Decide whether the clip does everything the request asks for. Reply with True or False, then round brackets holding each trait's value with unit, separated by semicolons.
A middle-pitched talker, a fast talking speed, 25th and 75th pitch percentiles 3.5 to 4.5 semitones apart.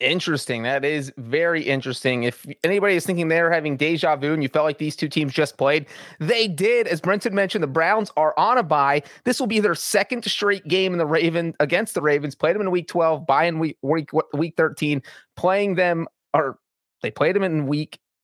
True (160 Hz; 215 wpm; 3.8 semitones)